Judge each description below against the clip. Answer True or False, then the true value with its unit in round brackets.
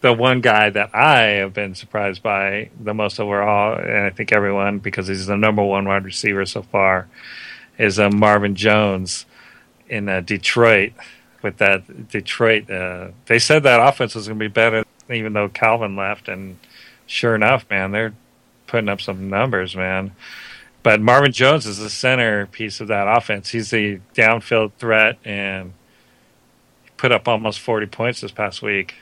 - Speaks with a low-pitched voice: True (105 Hz)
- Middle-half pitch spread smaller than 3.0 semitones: True (2.4 semitones)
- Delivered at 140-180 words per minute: True (165 wpm)